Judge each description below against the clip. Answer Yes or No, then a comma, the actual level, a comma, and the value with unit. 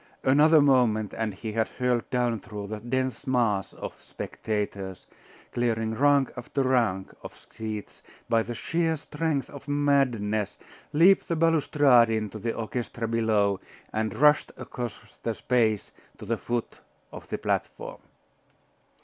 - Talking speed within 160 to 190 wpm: No, slow, 135 wpm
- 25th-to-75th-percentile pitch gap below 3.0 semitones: No, average, 4.0 semitones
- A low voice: Yes, low, 120 Hz